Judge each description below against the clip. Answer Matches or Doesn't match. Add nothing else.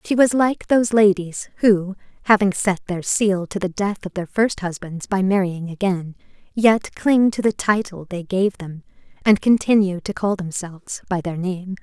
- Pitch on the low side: Doesn't match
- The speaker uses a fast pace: Doesn't match